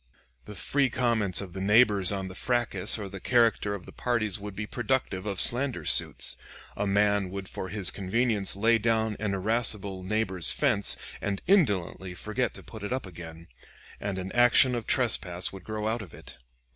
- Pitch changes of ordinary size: Yes, average, 3.5 semitones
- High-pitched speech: No, low, 105 Hz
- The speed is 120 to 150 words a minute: No, average, 185 wpm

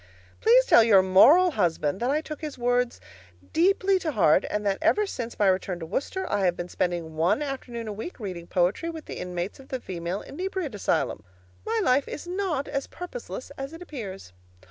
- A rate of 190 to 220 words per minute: Yes, average, 195 wpm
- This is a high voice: Yes, high, 240 Hz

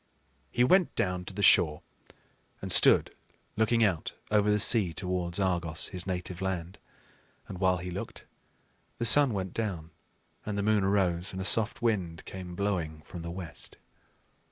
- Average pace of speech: Yes, average, 160 wpm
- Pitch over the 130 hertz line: No, very low, 95 Hz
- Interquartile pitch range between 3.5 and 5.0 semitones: No, average, 3.1 semitones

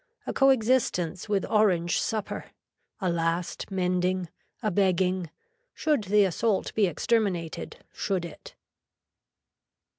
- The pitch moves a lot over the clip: No, average, 3.3 semitones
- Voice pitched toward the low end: No, medium, 185 Hz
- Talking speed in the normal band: No, slow, 110 wpm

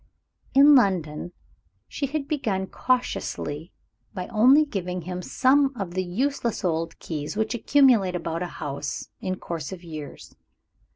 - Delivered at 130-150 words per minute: Yes, slow, 135 wpm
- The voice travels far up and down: Yes, wide, 7.2 semitones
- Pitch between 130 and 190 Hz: Yes, medium, 185 Hz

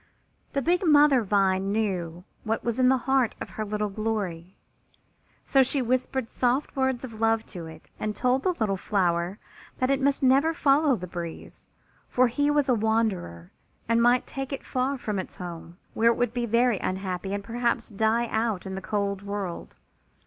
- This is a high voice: Yes, high, 225 Hz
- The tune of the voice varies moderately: Yes, average, 4.8 semitones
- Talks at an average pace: Yes, average, 185 wpm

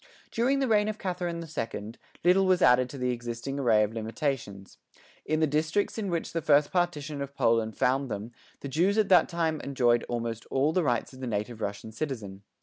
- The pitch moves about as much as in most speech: No, wide, 6.4 semitones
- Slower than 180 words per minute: No, fast, 205 wpm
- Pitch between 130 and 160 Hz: Yes, medium, 140 Hz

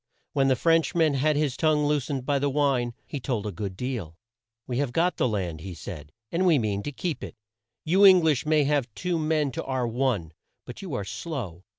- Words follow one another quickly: Yes, fast, 220 wpm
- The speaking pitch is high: No, low, 135 Hz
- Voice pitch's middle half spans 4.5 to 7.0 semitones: Yes, average, 5.2 semitones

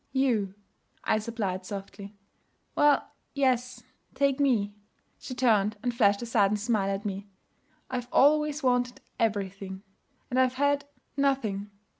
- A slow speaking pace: Yes, slow, 125 wpm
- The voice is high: Yes, high, 230 Hz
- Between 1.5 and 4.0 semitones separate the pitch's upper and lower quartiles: No, average, 4.6 semitones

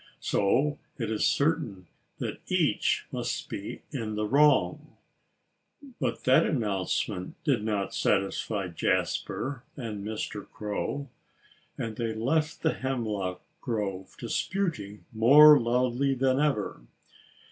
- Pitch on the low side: Yes, low, 115 Hz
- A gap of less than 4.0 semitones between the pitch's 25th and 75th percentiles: No, average, 5.0 semitones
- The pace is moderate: No, slow, 110 wpm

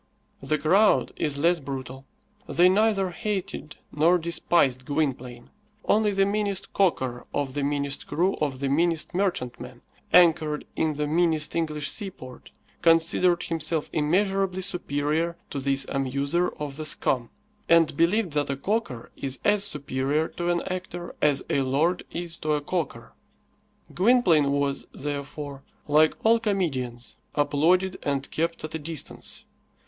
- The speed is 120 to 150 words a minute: Yes, average, 140 wpm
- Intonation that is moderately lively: Yes, average, 4.1 semitones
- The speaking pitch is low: No, medium, 155 Hz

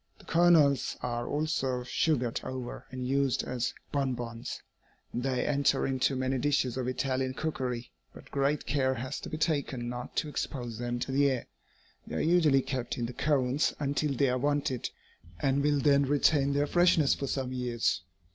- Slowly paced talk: No, average, 170 wpm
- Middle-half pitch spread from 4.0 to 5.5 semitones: No, narrow, 2.5 semitones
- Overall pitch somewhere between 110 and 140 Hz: Yes, low, 135 Hz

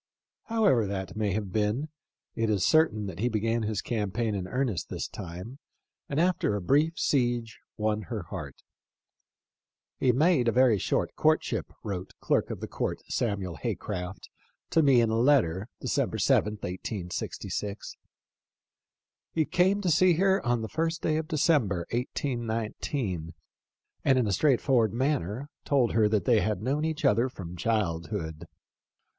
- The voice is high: No, low, 115 Hz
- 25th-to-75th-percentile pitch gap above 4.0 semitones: Yes, wide, 5.4 semitones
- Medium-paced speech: Yes, average, 145 wpm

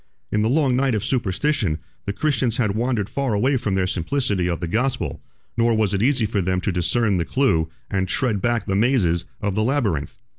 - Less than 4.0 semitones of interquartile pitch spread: No, average, 5.2 semitones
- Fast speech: Yes, fast, 210 wpm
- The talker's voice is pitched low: Yes, low, 110 Hz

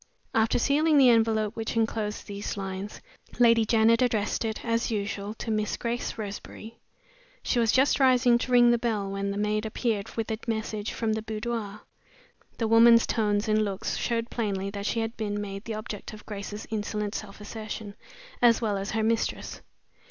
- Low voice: No, high, 220 Hz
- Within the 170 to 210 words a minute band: Yes, average, 180 wpm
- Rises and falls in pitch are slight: Yes, narrow, 1.8 semitones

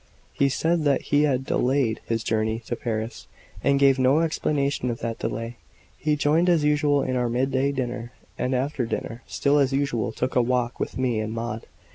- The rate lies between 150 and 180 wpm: No, average, 190 wpm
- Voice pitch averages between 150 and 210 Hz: No, low, 130 Hz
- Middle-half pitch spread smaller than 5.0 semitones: Yes, average, 3.2 semitones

